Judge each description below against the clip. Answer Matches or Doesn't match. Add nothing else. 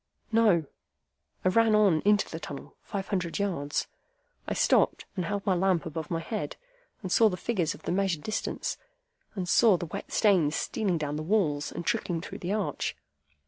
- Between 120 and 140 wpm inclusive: Doesn't match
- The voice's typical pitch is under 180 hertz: Doesn't match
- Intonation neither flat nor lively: Matches